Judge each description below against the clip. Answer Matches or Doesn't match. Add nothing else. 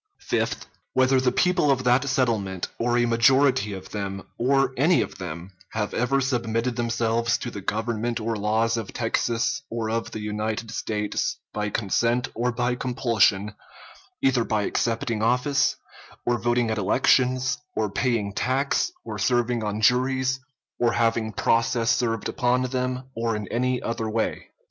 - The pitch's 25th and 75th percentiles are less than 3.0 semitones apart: Matches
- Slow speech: Doesn't match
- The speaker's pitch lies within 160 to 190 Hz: Doesn't match